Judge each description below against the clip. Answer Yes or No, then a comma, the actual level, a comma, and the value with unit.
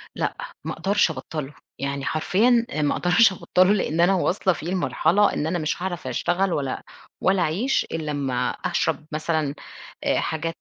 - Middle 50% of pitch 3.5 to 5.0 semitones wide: Yes, average, 3.9 semitones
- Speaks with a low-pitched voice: No, medium, 165 Hz